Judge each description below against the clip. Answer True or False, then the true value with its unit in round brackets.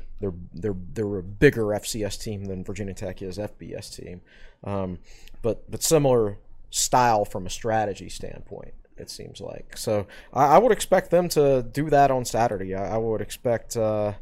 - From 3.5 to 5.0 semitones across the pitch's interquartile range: False (2.9 semitones)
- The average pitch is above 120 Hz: False (105 Hz)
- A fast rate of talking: False (175 wpm)